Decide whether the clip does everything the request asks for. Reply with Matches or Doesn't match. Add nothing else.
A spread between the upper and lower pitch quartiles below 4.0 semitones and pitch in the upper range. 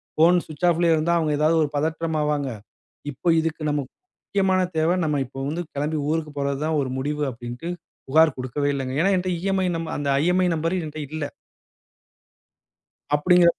Doesn't match